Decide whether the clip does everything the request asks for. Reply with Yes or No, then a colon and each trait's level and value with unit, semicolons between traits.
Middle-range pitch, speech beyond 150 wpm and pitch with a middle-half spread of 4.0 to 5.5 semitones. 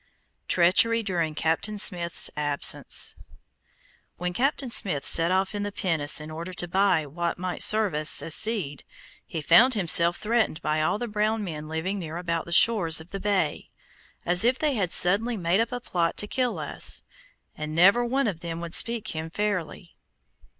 Yes: medium, 180 Hz; average, 180 wpm; average, 4.7 semitones